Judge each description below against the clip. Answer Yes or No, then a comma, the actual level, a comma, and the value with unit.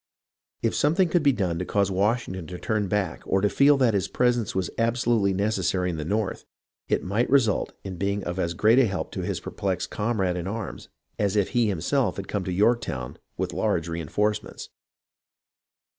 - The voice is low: Yes, low, 100 Hz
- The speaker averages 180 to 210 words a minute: Yes, average, 185 wpm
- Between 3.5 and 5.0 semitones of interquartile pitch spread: Yes, average, 4.0 semitones